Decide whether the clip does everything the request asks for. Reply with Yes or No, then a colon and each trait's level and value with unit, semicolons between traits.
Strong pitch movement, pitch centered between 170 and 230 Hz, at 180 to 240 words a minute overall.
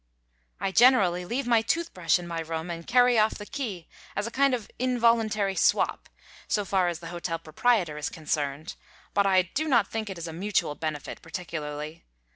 Yes: wide, 5.9 semitones; medium, 185 Hz; average, 190 wpm